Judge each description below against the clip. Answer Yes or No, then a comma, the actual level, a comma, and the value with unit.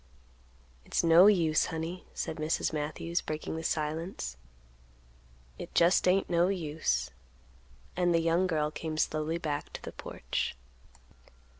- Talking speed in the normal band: No, slow, 130 wpm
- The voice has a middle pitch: Yes, medium, 160 Hz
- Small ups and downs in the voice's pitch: Yes, narrow, 2.0 semitones